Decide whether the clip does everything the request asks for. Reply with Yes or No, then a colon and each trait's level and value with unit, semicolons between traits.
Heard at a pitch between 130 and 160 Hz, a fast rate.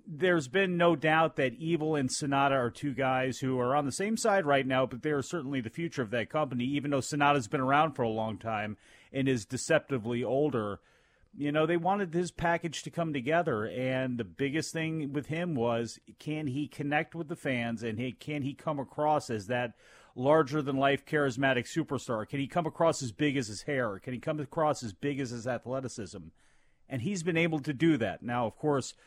Yes: medium, 140 Hz; fast, 210 wpm